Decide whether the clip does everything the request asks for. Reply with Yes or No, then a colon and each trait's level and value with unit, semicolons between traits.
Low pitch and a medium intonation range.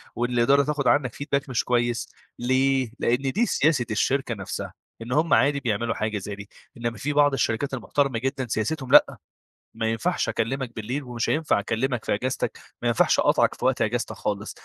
Yes: low, 125 Hz; average, 3.4 semitones